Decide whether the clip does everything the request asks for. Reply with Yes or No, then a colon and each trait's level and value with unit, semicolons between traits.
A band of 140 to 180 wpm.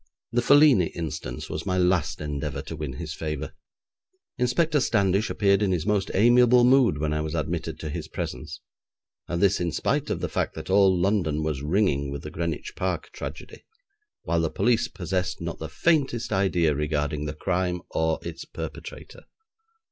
Yes: average, 170 wpm